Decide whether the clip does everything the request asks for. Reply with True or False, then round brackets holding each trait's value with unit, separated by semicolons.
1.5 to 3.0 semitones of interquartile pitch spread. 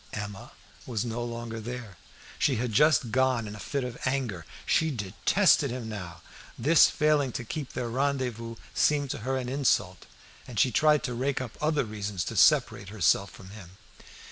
False (4.2 semitones)